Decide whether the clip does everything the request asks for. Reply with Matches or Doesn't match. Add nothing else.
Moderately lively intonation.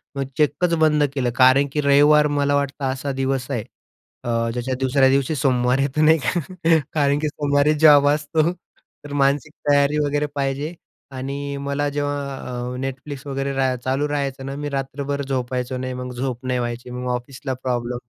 Doesn't match